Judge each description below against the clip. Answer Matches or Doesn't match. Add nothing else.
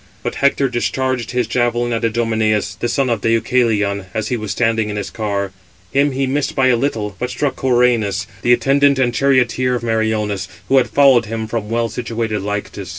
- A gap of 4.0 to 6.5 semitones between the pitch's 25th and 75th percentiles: Doesn't match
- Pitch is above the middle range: Doesn't match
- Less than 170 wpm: Doesn't match